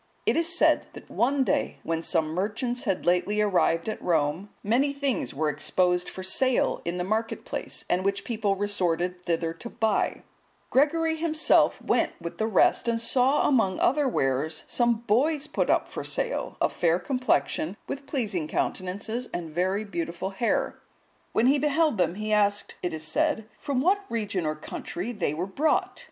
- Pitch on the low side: No, high, 205 Hz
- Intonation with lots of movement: Yes, wide, 6.5 semitones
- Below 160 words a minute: No, average, 170 wpm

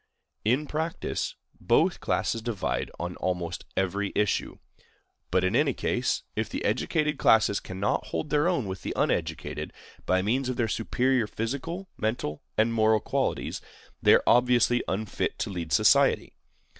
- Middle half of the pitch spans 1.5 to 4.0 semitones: No, average, 4.8 semitones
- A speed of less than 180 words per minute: Yes, average, 145 wpm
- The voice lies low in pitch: Yes, low, 110 Hz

